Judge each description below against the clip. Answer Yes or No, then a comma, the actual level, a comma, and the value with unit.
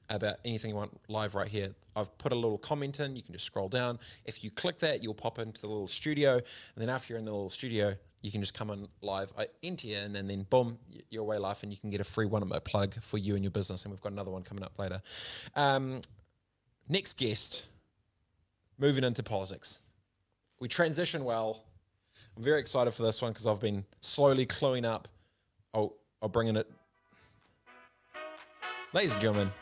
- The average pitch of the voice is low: Yes, low, 105 Hz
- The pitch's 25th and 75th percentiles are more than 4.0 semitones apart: No, average, 3.3 semitones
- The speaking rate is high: Yes, fast, 215 wpm